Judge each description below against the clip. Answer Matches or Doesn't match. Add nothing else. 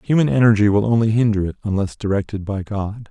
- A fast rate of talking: Doesn't match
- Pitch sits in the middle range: Doesn't match